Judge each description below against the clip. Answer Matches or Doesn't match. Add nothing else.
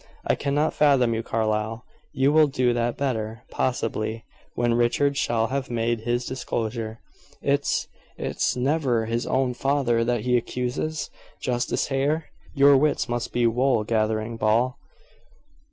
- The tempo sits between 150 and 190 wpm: Doesn't match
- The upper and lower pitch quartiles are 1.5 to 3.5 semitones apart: Matches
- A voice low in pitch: Matches